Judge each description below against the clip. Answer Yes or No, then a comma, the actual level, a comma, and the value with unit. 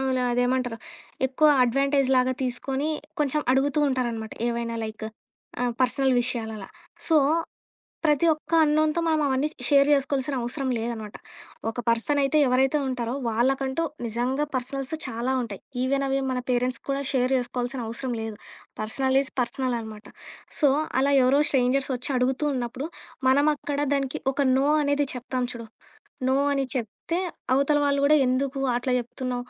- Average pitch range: No, narrow, 2.2 semitones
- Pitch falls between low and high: No, very high, 260 Hz